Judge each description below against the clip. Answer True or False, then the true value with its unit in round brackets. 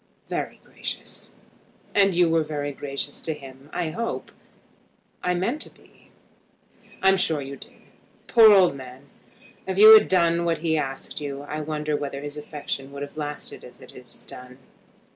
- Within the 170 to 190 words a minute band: False (160 wpm)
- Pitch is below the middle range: False (150 Hz)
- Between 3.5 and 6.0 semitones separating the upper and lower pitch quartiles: True (4.0 semitones)